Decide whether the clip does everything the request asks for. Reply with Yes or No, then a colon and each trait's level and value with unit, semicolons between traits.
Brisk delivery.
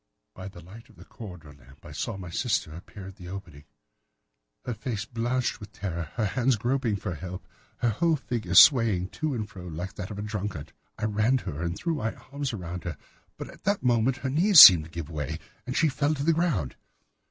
Yes: fast, 220 wpm